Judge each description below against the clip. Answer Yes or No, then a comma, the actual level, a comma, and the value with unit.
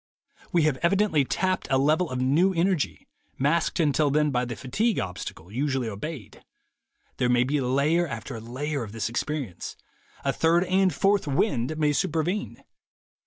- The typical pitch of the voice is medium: Yes, medium, 145 Hz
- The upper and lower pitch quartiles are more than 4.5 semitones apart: Yes, average, 5.2 semitones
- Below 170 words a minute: Yes, average, 155 wpm